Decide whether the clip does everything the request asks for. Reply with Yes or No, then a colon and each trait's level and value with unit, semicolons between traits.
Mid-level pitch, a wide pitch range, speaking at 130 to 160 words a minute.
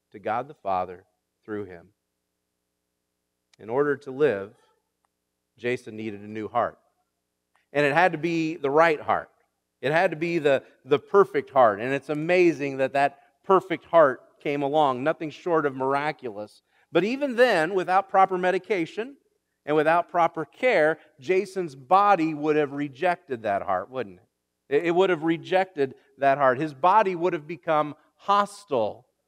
Yes: medium, 155 Hz; wide, 6.1 semitones; average, 155 wpm